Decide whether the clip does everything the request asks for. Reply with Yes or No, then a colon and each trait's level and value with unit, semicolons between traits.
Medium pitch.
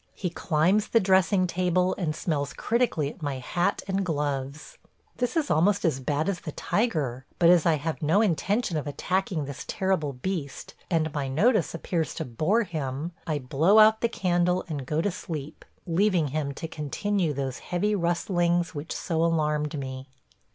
Yes: medium, 165 Hz